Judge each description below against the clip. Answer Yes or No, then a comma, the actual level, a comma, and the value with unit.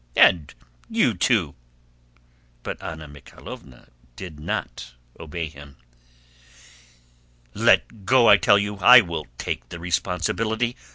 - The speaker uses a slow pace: Yes, slow, 110 wpm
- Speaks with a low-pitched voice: Yes, very low, 85 Hz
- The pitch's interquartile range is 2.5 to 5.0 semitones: No, wide, 5.4 semitones